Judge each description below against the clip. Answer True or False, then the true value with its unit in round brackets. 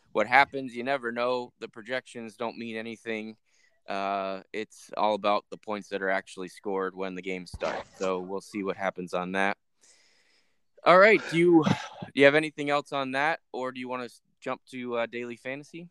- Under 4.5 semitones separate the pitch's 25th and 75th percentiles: False (5.3 semitones)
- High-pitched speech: False (115 Hz)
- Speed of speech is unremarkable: True (195 wpm)